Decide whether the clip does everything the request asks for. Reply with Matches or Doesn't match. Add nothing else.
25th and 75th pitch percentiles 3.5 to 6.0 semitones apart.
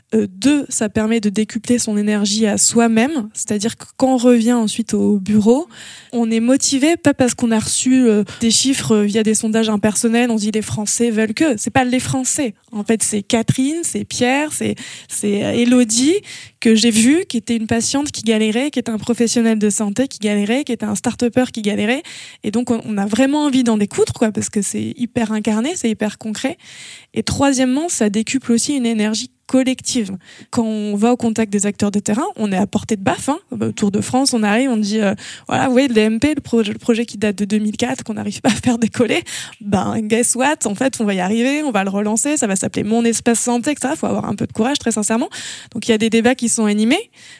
Doesn't match